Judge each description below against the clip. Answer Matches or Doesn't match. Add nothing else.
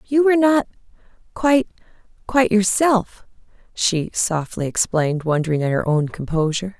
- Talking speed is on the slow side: Matches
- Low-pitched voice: Doesn't match